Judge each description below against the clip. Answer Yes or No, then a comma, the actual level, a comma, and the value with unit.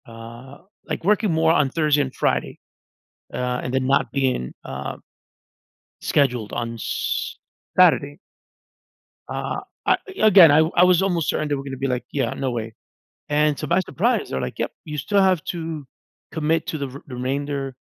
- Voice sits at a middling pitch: Yes, medium, 145 Hz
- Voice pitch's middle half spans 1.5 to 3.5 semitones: No, average, 4.2 semitones